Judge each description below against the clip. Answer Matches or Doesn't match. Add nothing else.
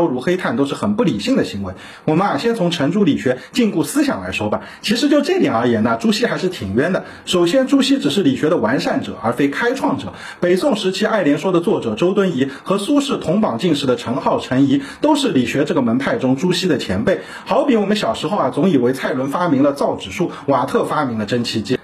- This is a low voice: Doesn't match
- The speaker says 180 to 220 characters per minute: Doesn't match